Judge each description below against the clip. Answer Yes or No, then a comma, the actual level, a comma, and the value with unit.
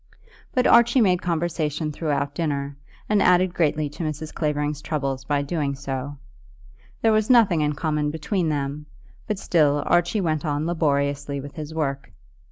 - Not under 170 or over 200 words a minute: No, average, 155 wpm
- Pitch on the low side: No, medium, 150 Hz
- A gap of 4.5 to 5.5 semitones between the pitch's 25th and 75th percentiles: No, average, 3.3 semitones